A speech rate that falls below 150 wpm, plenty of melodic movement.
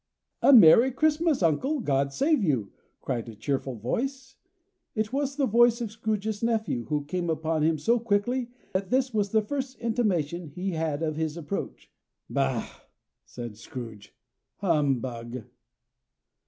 Yes: average, 140 wpm; wide, 8.7 semitones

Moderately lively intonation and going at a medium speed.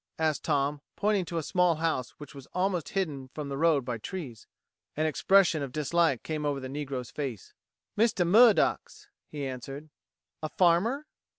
Yes: average, 4.5 semitones; average, 165 wpm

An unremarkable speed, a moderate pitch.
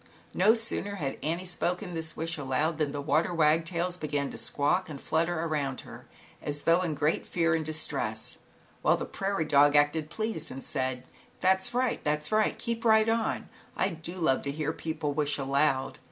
Yes: average, 185 wpm; medium, 160 Hz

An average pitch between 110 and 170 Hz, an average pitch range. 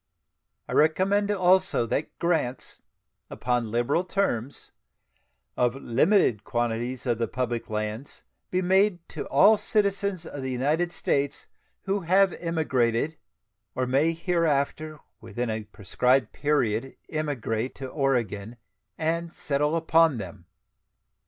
No: medium, 140 Hz; wide, 5.9 semitones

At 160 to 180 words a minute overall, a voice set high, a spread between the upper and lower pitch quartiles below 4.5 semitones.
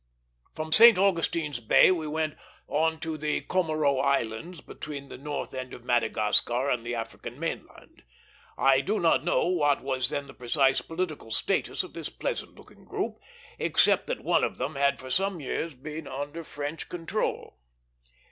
No: average, 165 wpm; medium, 145 Hz; average, 3.6 semitones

